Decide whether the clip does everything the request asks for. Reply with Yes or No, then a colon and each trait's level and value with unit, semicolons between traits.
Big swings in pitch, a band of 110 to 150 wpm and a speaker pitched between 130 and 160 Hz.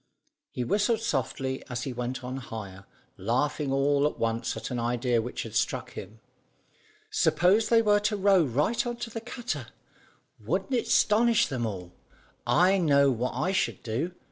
No: wide, 8.9 semitones; average, 165 wpm; low, 135 Hz